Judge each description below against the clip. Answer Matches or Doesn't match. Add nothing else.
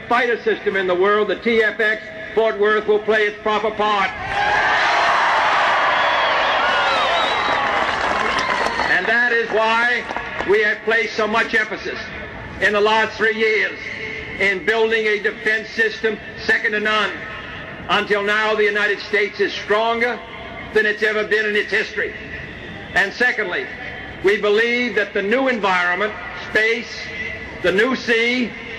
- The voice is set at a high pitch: Matches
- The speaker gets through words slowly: Matches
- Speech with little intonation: Matches